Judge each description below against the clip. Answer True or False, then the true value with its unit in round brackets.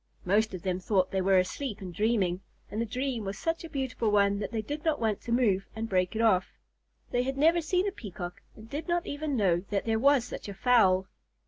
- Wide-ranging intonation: True (5.7 semitones)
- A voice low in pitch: False (220 Hz)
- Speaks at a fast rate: True (235 wpm)